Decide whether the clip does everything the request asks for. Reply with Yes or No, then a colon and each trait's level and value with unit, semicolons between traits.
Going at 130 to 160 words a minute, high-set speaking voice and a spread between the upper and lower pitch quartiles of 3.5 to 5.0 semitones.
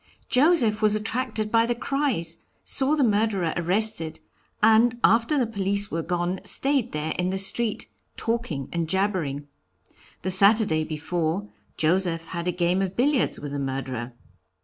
No: average, 150 wpm; high, 195 Hz; wide, 5.4 semitones